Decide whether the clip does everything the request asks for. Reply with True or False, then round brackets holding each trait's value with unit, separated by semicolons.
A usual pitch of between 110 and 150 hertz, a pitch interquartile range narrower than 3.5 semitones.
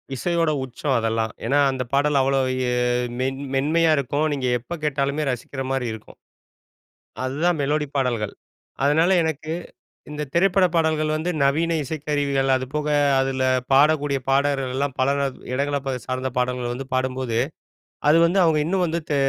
True (140 Hz; 2.9 semitones)